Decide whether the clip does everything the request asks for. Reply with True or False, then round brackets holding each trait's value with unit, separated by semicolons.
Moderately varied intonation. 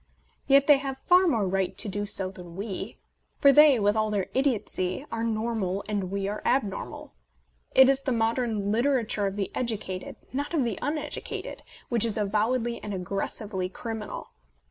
True (4.4 semitones)